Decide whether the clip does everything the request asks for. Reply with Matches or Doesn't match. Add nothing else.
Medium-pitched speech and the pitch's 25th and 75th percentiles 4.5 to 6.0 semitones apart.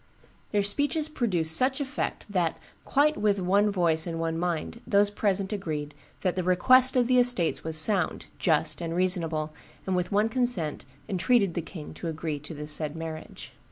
Matches